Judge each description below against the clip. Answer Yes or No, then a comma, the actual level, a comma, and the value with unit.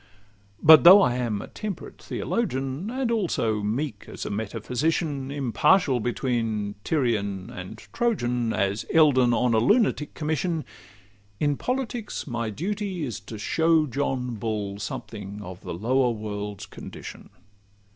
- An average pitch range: No, wide, 6.9 semitones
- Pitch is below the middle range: Yes, low, 125 Hz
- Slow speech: Yes, slow, 130 wpm